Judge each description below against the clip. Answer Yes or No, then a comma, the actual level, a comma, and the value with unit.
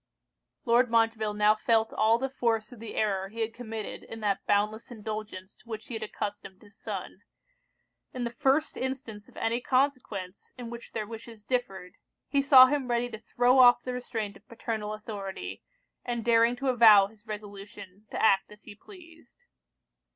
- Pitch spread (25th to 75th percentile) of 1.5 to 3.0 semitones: Yes, average, 2.7 semitones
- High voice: Yes, high, 225 Hz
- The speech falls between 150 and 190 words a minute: Yes, average, 175 wpm